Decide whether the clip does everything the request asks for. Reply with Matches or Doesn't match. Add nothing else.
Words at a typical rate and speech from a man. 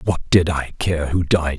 Doesn't match